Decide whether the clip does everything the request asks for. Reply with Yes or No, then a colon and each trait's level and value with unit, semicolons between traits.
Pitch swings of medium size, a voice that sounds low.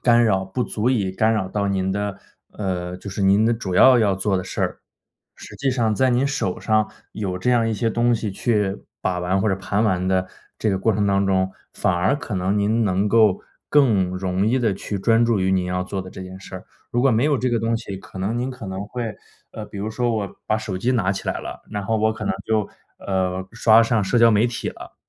Yes: average, 3.3 semitones; low, 105 Hz